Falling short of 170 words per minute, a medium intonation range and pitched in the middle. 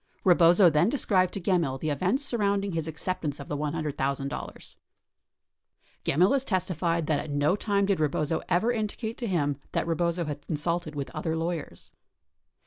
Yes: average, 155 wpm; average, 4.2 semitones; medium, 170 Hz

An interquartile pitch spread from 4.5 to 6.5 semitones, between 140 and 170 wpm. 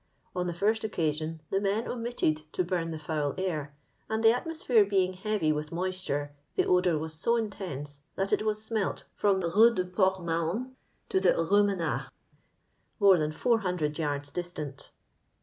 Yes: average, 4.9 semitones; average, 165 wpm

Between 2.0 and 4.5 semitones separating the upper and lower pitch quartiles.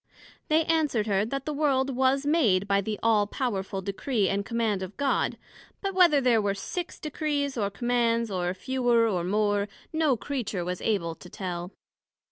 No: wide, 5.6 semitones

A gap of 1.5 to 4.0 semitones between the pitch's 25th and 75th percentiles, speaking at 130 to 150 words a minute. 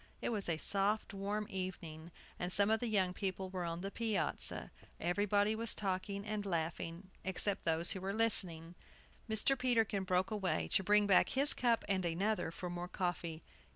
No: average, 3.0 semitones; average, 175 wpm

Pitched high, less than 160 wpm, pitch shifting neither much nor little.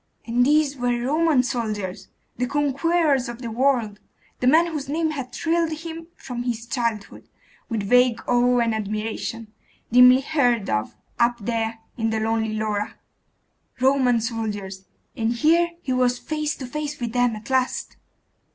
Yes: high, 245 Hz; average, 150 wpm; average, 3.8 semitones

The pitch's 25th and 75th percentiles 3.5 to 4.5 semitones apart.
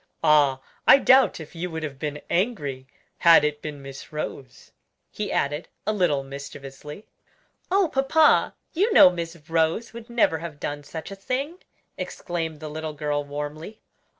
No: average, 5.2 semitones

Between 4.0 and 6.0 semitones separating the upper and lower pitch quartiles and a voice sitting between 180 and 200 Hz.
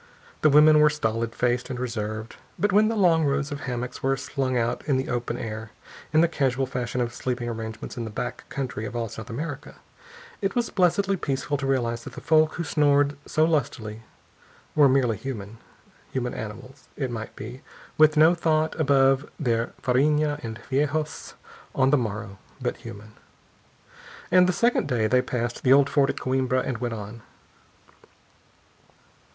No: average, 4.3 semitones; low, 130 Hz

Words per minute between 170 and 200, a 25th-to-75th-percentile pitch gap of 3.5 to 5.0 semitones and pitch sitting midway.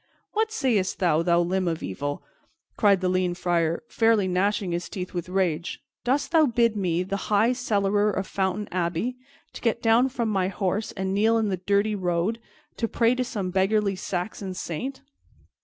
No: average, 175 wpm; average, 3.8 semitones; high, 195 Hz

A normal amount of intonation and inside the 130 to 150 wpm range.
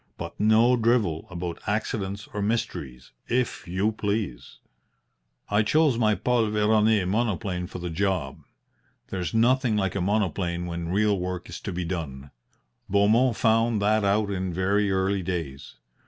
Yes: average, 3.5 semitones; average, 145 wpm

